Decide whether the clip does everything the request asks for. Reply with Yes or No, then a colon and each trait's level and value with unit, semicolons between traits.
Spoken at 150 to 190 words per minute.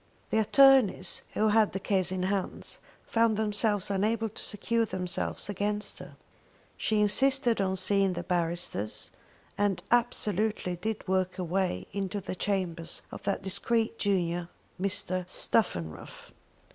No: slow, 135 wpm